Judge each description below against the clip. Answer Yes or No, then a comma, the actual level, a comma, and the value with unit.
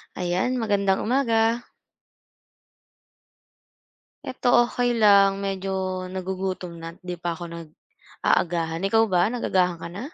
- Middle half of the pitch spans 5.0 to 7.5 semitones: No, average, 4.1 semitones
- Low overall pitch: No, high, 190 Hz